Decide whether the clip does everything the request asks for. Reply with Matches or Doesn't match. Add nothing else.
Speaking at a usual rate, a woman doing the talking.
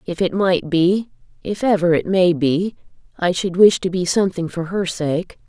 Matches